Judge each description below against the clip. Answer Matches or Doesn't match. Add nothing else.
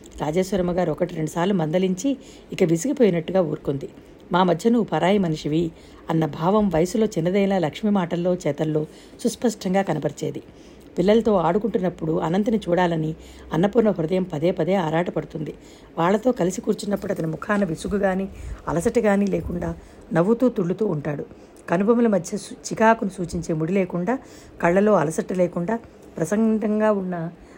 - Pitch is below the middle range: Doesn't match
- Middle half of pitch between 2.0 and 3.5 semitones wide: Doesn't match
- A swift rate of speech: Doesn't match